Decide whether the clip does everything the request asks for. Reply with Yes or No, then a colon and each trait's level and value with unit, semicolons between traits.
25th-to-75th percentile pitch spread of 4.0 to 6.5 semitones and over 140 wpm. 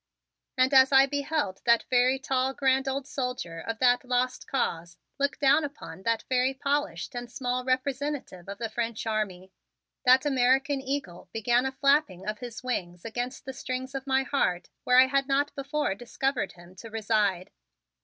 No: average, 3.3 semitones; average, 170 wpm